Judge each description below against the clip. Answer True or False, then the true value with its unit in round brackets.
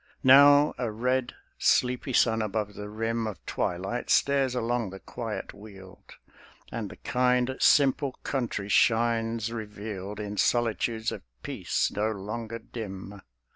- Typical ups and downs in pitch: True (3.1 semitones)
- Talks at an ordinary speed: False (130 wpm)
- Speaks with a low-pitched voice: True (115 Hz)